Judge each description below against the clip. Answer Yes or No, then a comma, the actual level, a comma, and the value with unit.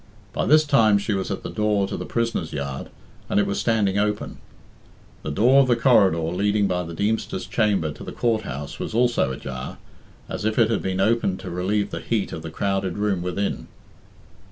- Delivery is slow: No, fast, 205 wpm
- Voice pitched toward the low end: Yes, low, 100 Hz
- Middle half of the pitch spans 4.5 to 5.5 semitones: No, average, 3.4 semitones